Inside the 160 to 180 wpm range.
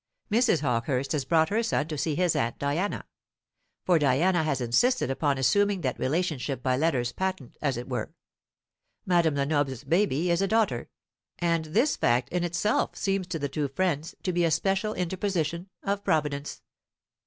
Yes: average, 165 wpm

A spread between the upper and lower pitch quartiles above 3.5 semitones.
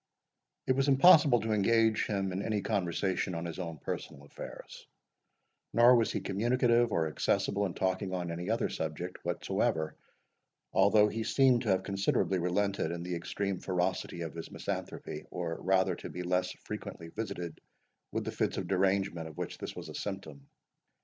Yes: average, 3.9 semitones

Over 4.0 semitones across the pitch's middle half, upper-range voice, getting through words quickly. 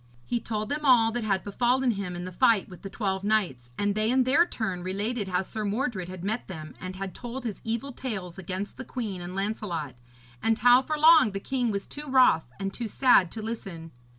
Yes: average, 4.5 semitones; high, 215 Hz; fast, 220 wpm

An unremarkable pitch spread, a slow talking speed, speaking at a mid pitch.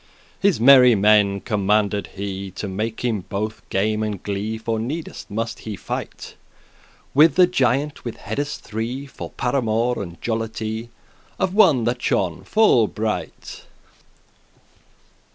No: average, 3.3 semitones; slow, 130 wpm; low, 110 Hz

